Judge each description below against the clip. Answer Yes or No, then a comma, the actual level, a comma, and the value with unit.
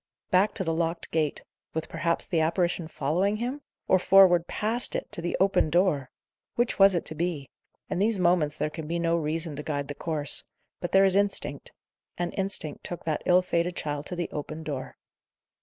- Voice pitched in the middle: Yes, medium, 170 Hz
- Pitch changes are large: No, average, 3.3 semitones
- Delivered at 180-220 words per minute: Yes, average, 195 wpm